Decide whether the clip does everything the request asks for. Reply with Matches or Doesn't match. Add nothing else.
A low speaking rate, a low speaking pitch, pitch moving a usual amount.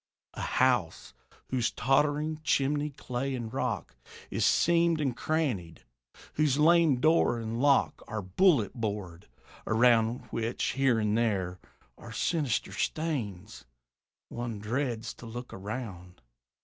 Matches